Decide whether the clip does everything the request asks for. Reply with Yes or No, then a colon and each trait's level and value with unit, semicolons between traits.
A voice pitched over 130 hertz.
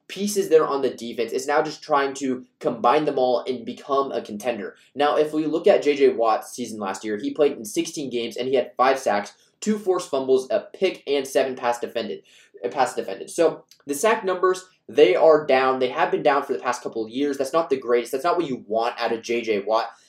Yes: medium, 140 Hz